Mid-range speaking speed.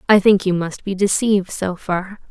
No: fast, 210 wpm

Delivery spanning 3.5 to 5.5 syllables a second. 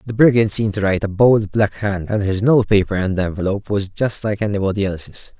No: 5.9 syllables/s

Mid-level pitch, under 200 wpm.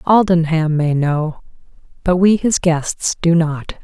Yes: medium, 165 Hz; average, 140 wpm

